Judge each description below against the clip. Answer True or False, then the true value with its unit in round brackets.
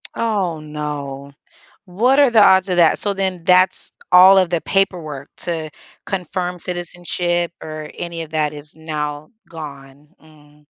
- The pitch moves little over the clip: False (3.4 semitones)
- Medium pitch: True (170 Hz)